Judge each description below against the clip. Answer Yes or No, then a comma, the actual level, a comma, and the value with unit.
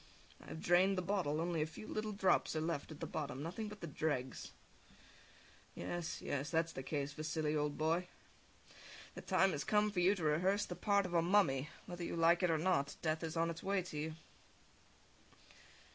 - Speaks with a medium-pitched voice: Yes, medium, 165 Hz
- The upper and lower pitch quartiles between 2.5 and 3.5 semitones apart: Yes, average, 3.2 semitones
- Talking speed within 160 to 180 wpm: No, average, 200 wpm